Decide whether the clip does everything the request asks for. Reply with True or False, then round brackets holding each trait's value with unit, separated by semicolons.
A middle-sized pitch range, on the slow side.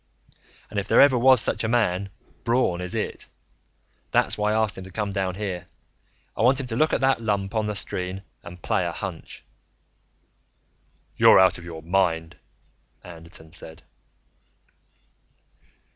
False (3.8 semitones; 160 wpm)